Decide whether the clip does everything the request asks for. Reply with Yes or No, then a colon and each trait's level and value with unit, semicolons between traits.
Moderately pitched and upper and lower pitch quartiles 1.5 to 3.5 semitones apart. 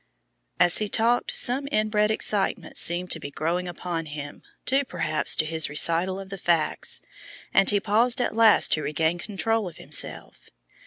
No: medium, 180 Hz; average, 4.7 semitones